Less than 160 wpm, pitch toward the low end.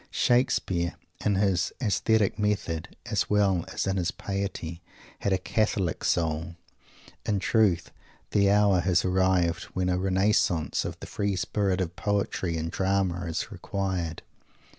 Yes: average, 140 wpm; very low, 95 Hz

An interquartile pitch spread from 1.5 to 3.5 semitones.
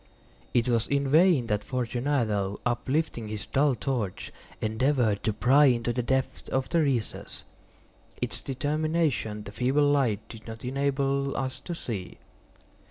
No: average, 4.0 semitones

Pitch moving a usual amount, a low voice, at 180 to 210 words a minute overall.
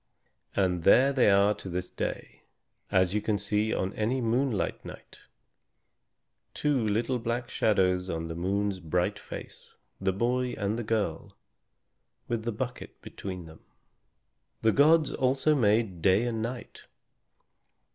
No: average, 4.3 semitones; low, 105 Hz; slow, 135 wpm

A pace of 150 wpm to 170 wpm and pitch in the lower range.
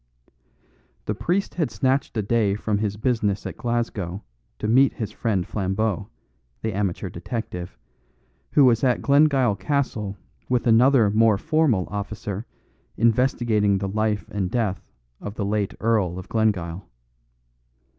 No: slow, 135 wpm; low, 110 Hz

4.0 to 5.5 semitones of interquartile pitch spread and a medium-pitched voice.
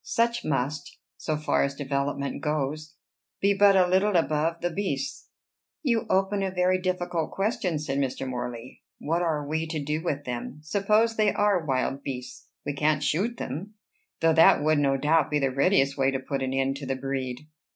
Yes: average, 5.1 semitones; medium, 150 Hz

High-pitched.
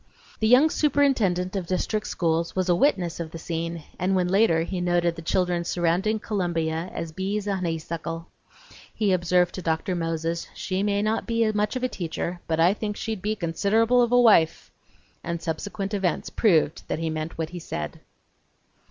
No: medium, 180 Hz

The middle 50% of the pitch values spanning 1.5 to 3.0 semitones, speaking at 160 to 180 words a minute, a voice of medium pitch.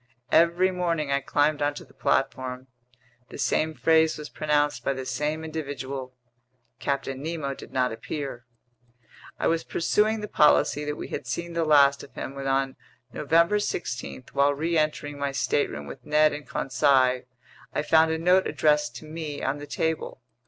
Yes: average, 2.7 semitones; average, 165 wpm; medium, 150 Hz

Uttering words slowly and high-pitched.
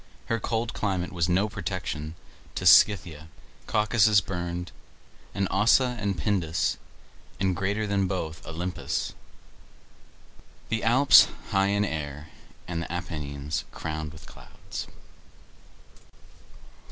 No: slow, 105 wpm; very low, 95 Hz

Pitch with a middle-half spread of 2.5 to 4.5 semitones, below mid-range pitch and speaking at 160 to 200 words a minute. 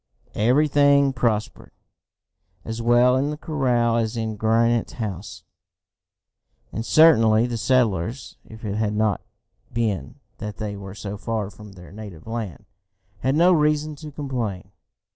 No: average, 4.0 semitones; low, 115 Hz; slow, 135 wpm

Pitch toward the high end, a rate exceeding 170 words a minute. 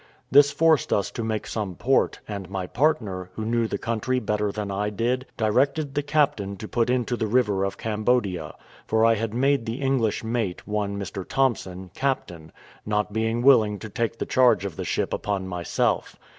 No: low, 110 Hz; average, 185 wpm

